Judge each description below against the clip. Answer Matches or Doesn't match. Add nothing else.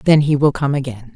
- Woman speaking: Matches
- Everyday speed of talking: Doesn't match